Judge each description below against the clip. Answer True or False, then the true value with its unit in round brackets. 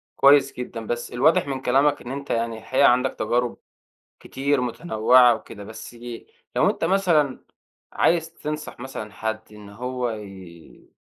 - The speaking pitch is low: True (125 Hz)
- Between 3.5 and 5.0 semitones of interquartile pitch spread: True (4.0 semitones)